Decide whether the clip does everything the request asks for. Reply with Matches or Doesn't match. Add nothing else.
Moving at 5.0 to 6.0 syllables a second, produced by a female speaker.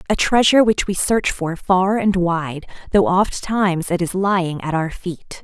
Doesn't match